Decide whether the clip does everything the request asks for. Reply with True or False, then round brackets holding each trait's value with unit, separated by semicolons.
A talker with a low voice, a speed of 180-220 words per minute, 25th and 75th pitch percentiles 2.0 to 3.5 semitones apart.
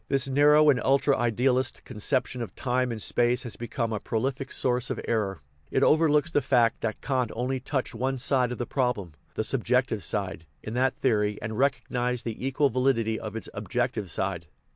True (125 Hz; 185 wpm; 3.0 semitones)